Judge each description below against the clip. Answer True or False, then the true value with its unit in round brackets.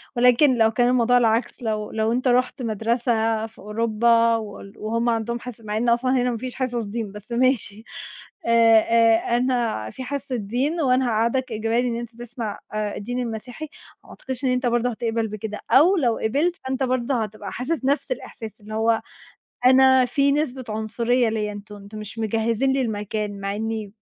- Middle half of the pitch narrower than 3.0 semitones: True (2.4 semitones)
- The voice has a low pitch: False (230 Hz)